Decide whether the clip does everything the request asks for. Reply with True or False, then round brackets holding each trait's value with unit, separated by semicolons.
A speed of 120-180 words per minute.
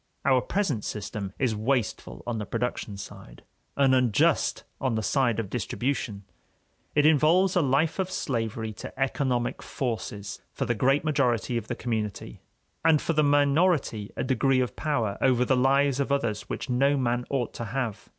True (170 wpm)